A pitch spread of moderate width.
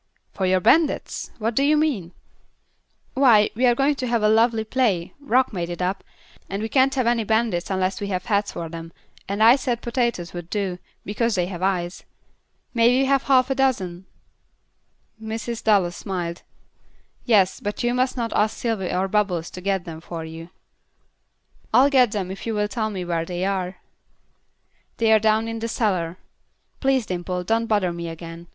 Yes: average, 4.7 semitones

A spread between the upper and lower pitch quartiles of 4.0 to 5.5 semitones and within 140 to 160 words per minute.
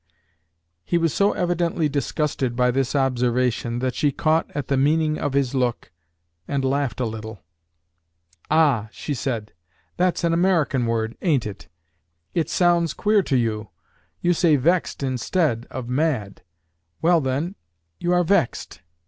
Yes: average, 5.2 semitones; average, 145 wpm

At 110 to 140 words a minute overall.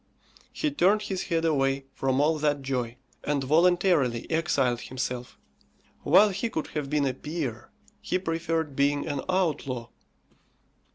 Yes: slow, 135 wpm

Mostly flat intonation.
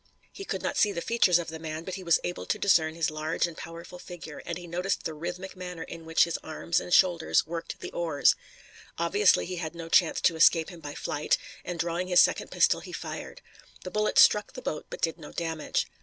Yes: narrow, 1.9 semitones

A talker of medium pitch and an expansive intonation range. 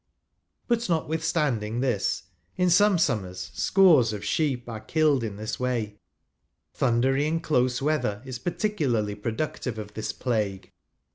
No: low, 125 Hz; wide, 6.3 semitones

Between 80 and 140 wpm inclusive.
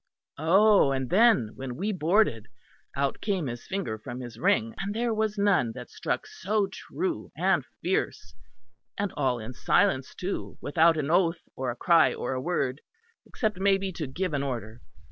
No: average, 170 wpm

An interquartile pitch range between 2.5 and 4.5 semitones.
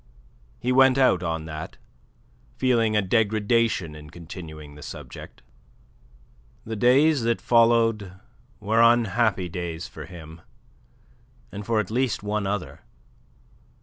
No: average, 5.1 semitones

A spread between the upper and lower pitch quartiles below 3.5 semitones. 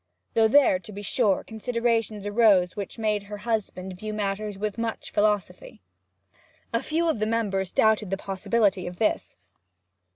Yes: narrow, 2.4 semitones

